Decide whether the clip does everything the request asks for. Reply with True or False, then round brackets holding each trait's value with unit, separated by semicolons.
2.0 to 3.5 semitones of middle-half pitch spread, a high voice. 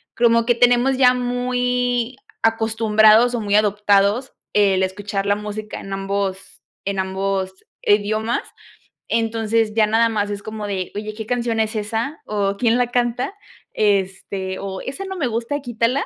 True (3.0 semitones; 220 Hz)